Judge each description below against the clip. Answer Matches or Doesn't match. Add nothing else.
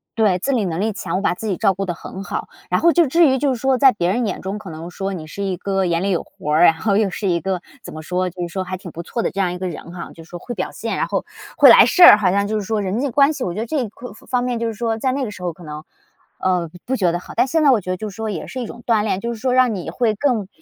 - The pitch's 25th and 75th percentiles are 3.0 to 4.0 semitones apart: Doesn't match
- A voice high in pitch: Matches